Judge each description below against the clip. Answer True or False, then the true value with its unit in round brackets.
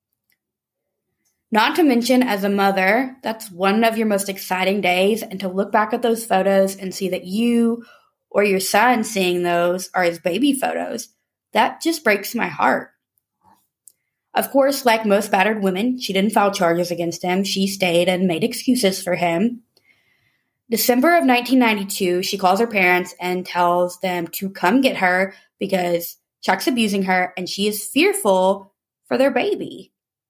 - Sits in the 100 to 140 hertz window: False (195 Hz)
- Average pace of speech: True (160 wpm)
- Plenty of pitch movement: False (4.1 semitones)